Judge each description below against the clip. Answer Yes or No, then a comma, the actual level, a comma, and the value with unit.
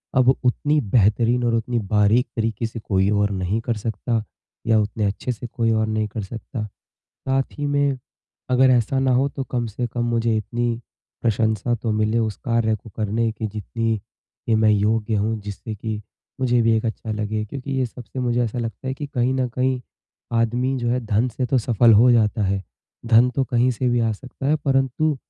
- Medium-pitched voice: No, low, 115 Hz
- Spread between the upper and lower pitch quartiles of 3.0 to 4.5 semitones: No, narrow, 2.5 semitones